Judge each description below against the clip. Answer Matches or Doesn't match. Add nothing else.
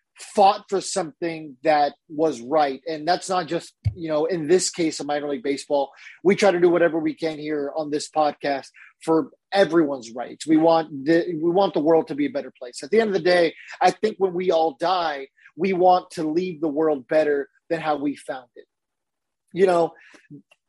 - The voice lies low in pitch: Doesn't match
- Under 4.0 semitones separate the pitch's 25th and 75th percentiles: Matches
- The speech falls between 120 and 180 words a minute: Doesn't match